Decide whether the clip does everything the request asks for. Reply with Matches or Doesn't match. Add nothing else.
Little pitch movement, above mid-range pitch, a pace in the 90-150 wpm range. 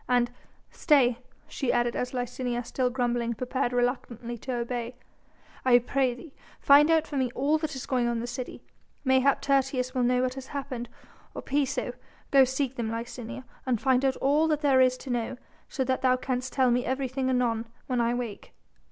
Doesn't match